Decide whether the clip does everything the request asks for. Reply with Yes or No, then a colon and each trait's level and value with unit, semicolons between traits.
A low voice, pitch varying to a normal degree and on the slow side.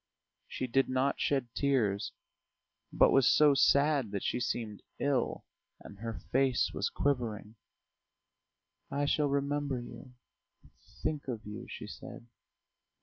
Yes: low, 130 Hz; average, 3.6 semitones; slow, 125 wpm